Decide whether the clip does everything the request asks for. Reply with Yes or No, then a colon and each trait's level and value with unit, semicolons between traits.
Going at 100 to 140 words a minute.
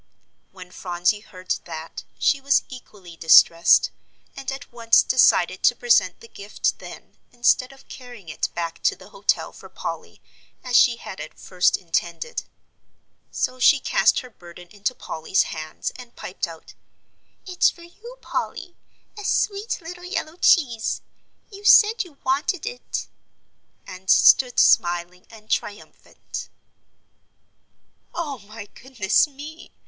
Yes: slow, 135 wpm